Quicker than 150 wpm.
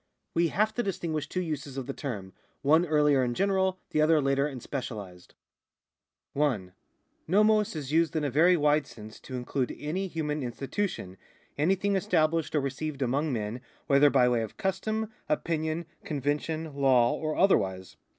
Yes: average, 160 wpm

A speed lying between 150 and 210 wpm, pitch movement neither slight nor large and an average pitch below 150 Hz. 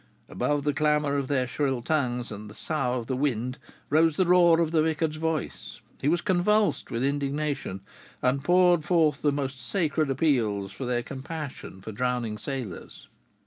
Yes: average, 170 wpm; average, 4.1 semitones; medium, 140 Hz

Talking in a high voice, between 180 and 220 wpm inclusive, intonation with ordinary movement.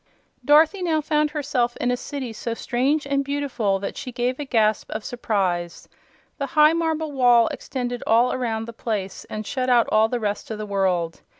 Yes: high, 245 Hz; average, 190 wpm; average, 4.7 semitones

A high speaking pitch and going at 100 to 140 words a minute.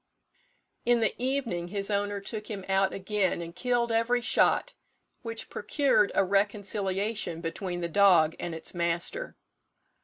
Yes: high, 200 Hz; slow, 135 wpm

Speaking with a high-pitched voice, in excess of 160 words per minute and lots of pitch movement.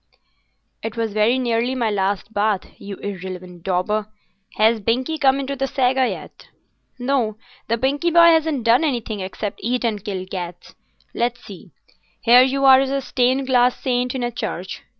No: high, 240 Hz; average, 170 wpm; average, 4.2 semitones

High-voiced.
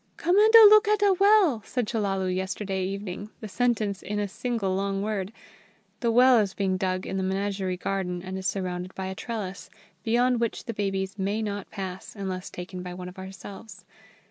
Yes: high, 195 Hz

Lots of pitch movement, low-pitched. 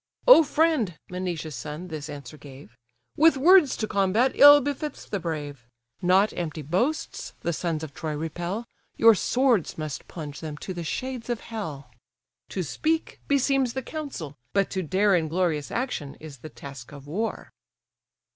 No: wide, 8.5 semitones; medium, 180 Hz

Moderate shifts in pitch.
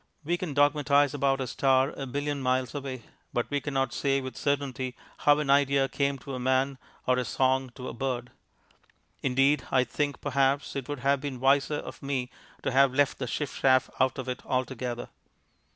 No: narrow, 1.6 semitones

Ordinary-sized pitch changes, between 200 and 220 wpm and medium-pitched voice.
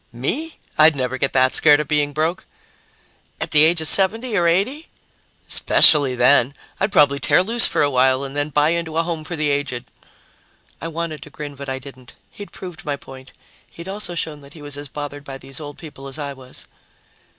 Yes: average, 3.5 semitones; fast, 205 wpm; medium, 150 Hz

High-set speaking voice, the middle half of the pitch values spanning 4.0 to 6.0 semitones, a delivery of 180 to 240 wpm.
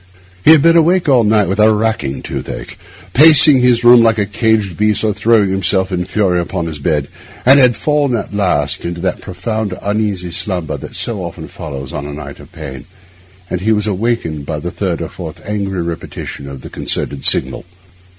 No: low, 100 Hz; average, 5.0 semitones; average, 190 wpm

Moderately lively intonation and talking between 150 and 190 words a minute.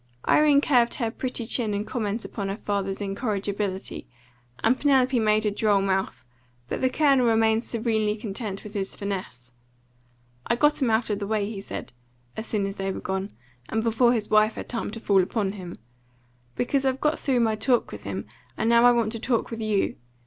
No: average, 3.1 semitones; average, 200 wpm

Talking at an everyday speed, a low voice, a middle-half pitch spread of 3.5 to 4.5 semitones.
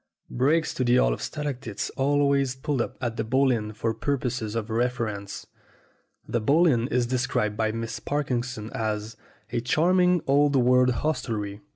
Yes: average, 160 wpm; low, 125 Hz; average, 3.8 semitones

